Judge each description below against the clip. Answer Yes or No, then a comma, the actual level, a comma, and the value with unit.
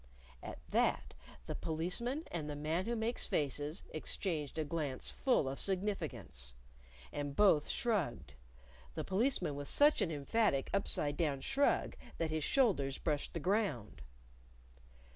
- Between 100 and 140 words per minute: Yes, slow, 135 wpm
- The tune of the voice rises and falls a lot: Yes, wide, 6.2 semitones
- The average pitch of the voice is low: No, medium, 160 Hz